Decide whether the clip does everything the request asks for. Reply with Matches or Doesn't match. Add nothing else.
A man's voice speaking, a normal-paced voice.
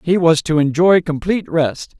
Matches